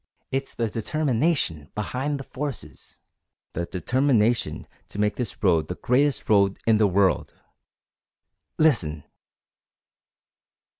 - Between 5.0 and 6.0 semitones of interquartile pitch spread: Yes, wide, 5.6 semitones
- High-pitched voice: No, low, 115 Hz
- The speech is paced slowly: Yes, slow, 105 wpm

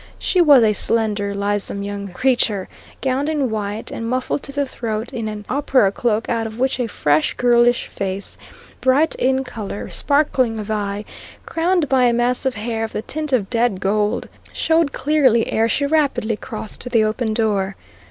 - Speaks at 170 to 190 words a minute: Yes, average, 180 wpm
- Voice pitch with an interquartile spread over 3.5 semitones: Yes, average, 3.9 semitones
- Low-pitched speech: No, high, 230 Hz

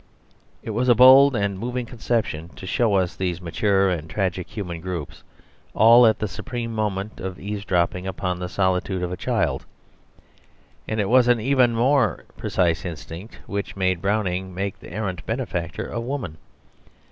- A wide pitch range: No, average, 4.3 semitones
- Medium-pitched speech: No, low, 100 Hz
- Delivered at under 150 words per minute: No, average, 160 wpm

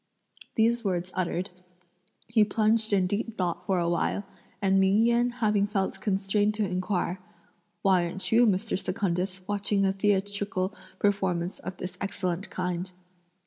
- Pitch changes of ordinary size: No, narrow, 2.3 semitones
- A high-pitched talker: Yes, high, 195 Hz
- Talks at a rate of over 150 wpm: No, average, 145 wpm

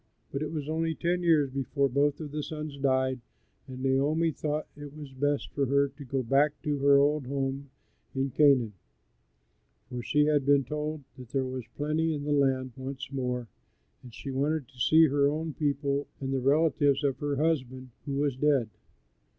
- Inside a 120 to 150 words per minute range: No, average, 185 wpm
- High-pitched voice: No, medium, 140 Hz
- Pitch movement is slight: Yes, narrow, 2.0 semitones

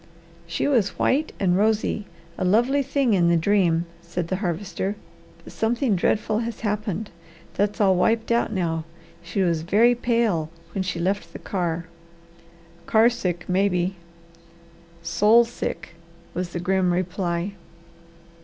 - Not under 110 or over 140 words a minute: Yes, slow, 135 wpm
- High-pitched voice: Yes, high, 195 Hz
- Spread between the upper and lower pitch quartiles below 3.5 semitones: No, average, 4.1 semitones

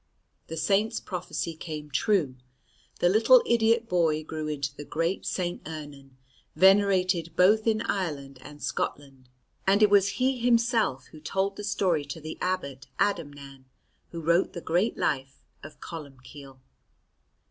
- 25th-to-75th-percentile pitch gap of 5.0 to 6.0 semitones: Yes, wide, 5.5 semitones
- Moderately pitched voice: Yes, medium, 165 Hz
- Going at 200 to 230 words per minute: No, average, 140 wpm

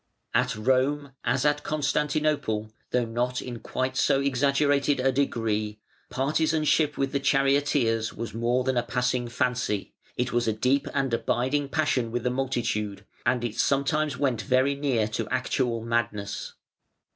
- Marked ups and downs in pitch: No, average, 3.2 semitones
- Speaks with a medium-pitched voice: No, low, 130 Hz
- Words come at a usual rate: Yes, average, 150 wpm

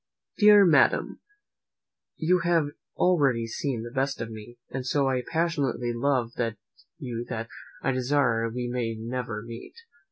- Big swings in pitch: No, average, 3.7 semitones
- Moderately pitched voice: No, low, 125 Hz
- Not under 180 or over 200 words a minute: No, slow, 135 wpm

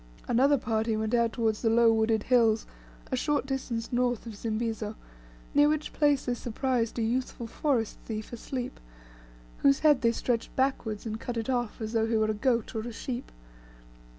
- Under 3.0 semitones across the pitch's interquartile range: Yes, narrow, 2.6 semitones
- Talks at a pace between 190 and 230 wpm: No, average, 180 wpm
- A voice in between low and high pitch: No, high, 235 Hz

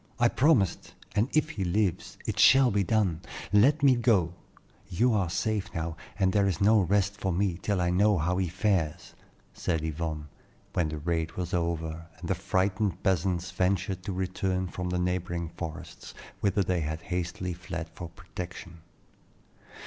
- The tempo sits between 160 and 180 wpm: Yes, average, 165 wpm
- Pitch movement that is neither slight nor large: Yes, average, 3.0 semitones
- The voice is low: Yes, very low, 90 Hz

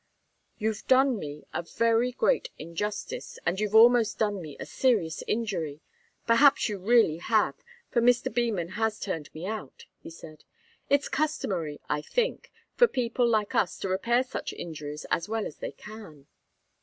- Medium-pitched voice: No, high, 215 Hz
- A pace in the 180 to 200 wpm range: No, average, 160 wpm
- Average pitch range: No, wide, 6.0 semitones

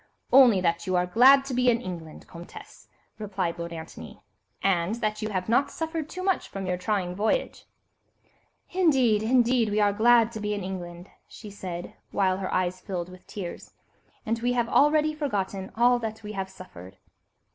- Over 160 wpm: Yes, average, 180 wpm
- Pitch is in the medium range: No, high, 210 Hz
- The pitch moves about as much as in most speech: Yes, average, 4.7 semitones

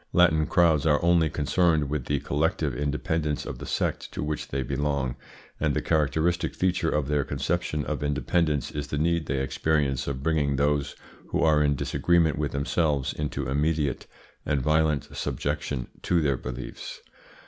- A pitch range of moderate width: No, narrow, 2.1 semitones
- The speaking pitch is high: No, very low, 75 Hz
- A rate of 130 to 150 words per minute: No, average, 160 wpm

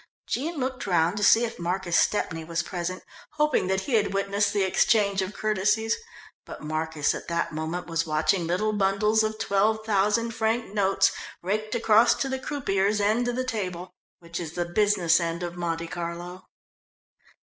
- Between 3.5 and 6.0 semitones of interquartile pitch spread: Yes, average, 4.0 semitones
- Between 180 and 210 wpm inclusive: No, average, 170 wpm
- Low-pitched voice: No, high, 195 Hz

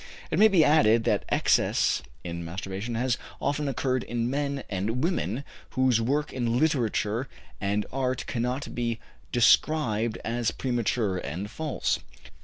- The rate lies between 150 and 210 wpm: No, slow, 135 wpm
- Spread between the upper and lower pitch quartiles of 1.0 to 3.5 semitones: No, average, 4.0 semitones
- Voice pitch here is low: Yes, low, 120 Hz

